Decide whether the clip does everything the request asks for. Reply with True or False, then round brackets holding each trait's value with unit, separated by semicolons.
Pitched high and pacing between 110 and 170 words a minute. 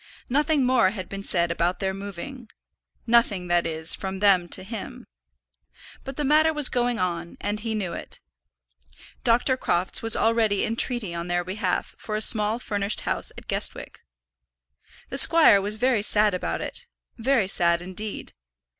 True (210 Hz; 165 wpm)